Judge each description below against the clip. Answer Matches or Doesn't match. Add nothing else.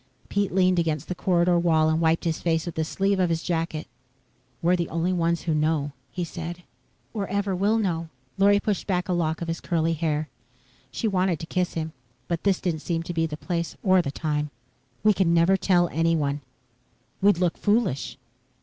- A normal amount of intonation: Doesn't match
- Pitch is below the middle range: Doesn't match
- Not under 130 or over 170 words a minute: Doesn't match